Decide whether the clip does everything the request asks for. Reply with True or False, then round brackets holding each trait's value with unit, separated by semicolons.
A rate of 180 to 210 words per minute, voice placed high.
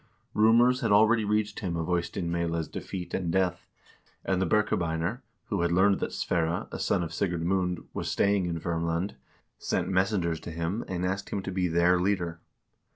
False (185 wpm; 90 Hz)